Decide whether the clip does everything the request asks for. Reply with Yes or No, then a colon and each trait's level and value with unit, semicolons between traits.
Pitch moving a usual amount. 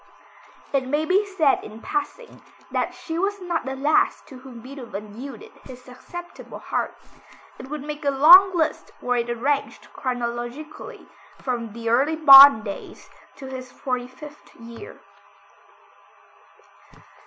Yes: average, 4.1 semitones